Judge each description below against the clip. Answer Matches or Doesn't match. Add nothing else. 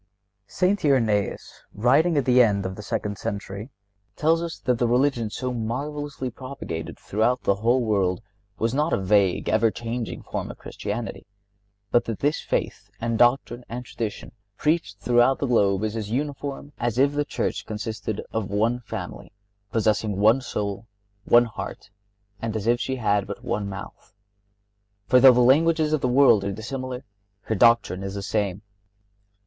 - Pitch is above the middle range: Doesn't match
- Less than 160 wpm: Doesn't match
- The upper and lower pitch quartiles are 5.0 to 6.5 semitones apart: Doesn't match